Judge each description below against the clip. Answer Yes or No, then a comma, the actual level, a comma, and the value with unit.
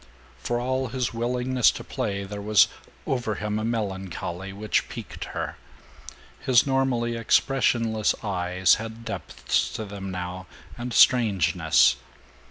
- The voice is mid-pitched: No, low, 110 Hz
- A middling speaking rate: No, slow, 125 wpm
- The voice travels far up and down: No, average, 3.6 semitones